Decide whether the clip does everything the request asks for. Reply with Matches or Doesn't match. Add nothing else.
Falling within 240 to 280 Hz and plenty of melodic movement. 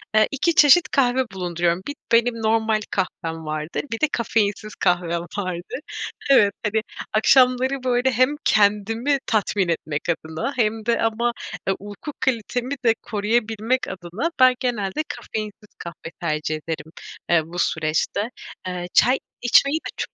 Doesn't match